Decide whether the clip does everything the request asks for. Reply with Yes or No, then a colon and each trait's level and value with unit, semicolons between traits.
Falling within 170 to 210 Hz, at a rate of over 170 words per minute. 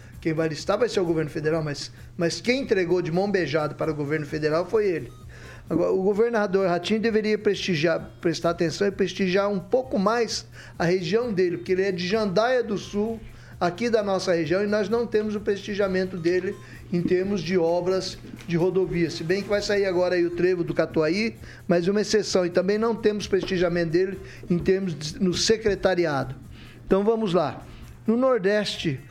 Yes: medium, 185 Hz; fast, 185 wpm